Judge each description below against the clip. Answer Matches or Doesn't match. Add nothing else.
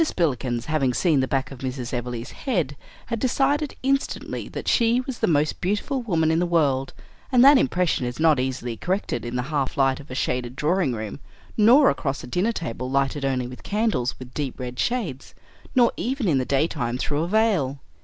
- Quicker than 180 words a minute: Matches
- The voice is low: Doesn't match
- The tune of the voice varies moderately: Doesn't match